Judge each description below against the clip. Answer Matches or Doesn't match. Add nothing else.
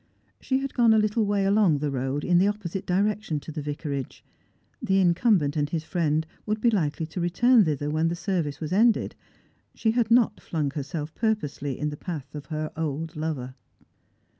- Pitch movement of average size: Doesn't match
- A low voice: Doesn't match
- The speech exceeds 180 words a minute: Matches